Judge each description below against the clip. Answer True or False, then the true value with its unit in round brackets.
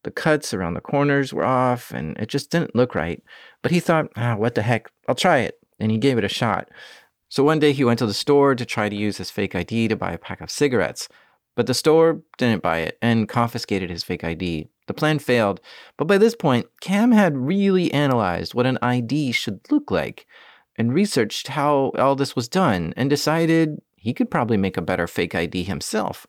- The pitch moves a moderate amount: False (5.8 semitones)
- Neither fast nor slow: False (220 wpm)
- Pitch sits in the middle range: False (125 Hz)